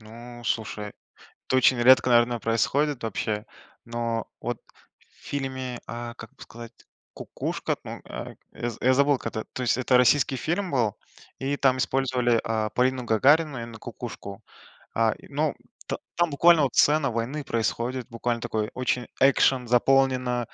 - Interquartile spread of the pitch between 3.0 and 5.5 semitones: No, narrow, 2.5 semitones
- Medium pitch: No, low, 125 Hz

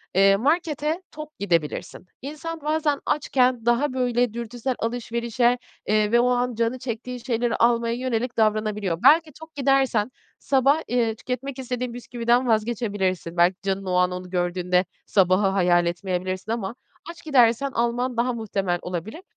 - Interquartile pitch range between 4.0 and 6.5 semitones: Yes, average, 4.6 semitones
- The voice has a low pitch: No, high, 235 Hz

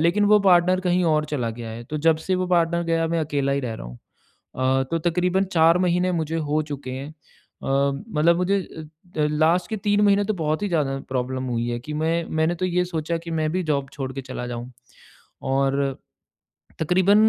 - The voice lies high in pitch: No, medium, 160 Hz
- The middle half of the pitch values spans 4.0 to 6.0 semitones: Yes, average, 4.7 semitones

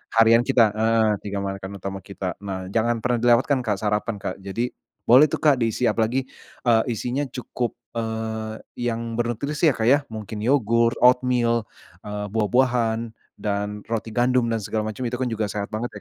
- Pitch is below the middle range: Yes, low, 115 Hz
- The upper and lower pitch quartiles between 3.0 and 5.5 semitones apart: No, narrow, 2.6 semitones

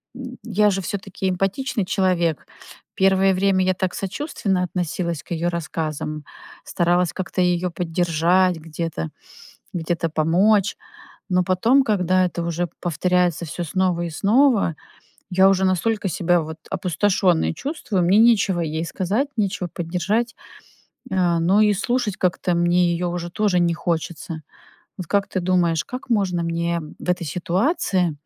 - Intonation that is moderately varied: No, narrow, 2.3 semitones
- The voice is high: No, medium, 180 Hz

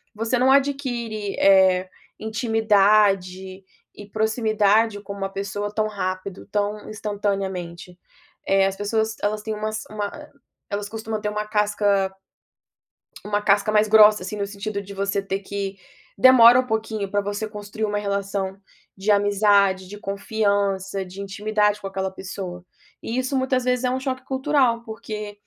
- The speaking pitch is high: Yes, high, 205 Hz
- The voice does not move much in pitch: Yes, narrow, 1.7 semitones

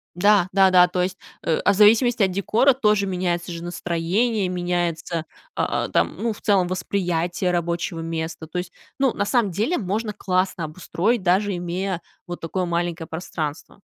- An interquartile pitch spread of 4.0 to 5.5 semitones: No, average, 2.8 semitones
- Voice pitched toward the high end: No, medium, 180 Hz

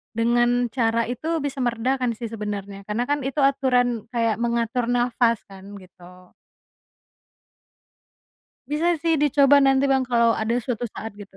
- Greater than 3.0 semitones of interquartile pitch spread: No, average, 2.7 semitones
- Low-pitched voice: No, high, 240 Hz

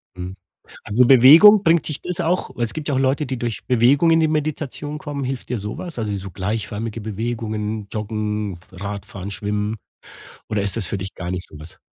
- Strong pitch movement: Yes, wide, 5.8 semitones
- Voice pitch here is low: Yes, low, 115 Hz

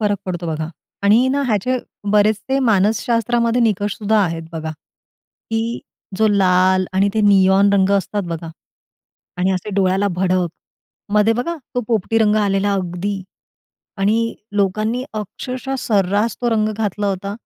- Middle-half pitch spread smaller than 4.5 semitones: Yes, average, 2.9 semitones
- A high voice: Yes, high, 205 Hz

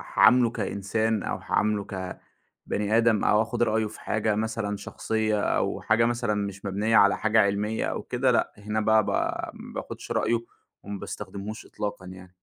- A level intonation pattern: Yes, narrow, 1.7 semitones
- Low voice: Yes, low, 105 Hz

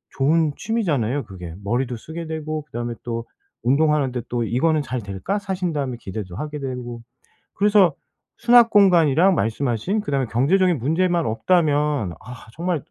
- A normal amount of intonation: No, wide, 6.3 semitones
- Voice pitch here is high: No, medium, 145 Hz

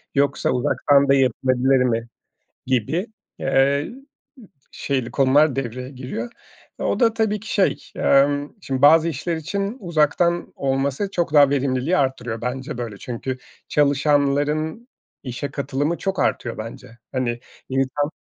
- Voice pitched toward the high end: No, medium, 140 Hz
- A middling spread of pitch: Yes, average, 3.4 semitones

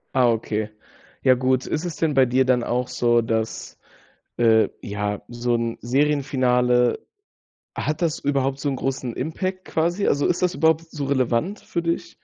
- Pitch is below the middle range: Yes, low, 130 Hz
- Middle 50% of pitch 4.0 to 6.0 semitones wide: Yes, average, 4.3 semitones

